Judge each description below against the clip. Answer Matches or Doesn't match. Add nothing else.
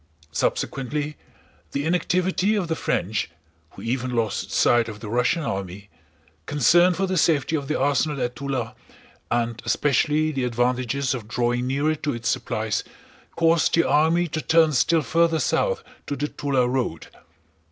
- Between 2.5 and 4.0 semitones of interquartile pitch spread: Doesn't match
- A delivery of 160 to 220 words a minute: Doesn't match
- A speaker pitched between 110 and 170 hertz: Matches